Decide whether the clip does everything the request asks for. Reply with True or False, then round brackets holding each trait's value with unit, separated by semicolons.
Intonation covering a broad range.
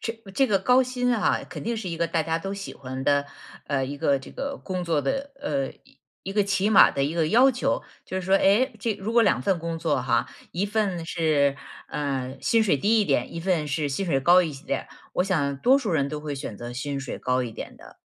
True (6.6 semitones)